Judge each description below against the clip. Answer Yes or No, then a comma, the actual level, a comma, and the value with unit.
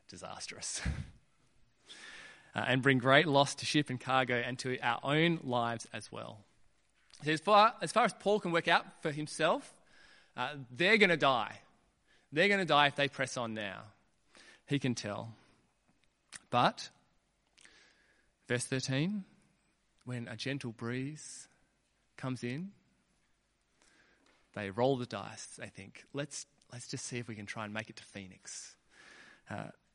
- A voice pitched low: Yes, low, 130 Hz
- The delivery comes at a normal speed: Yes, average, 150 wpm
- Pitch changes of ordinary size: Yes, average, 4.0 semitones